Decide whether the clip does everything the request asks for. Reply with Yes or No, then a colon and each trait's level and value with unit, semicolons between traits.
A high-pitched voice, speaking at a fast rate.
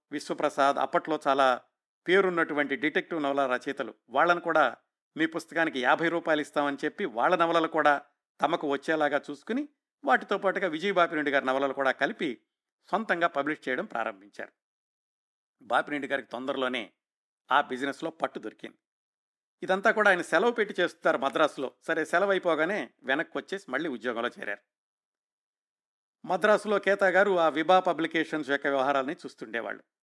No: medium, 155 Hz; fast, 130 wpm